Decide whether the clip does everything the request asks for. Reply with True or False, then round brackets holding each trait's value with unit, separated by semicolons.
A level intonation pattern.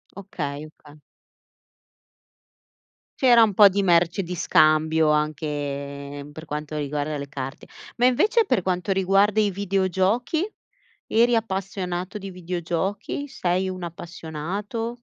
False (4.7 semitones)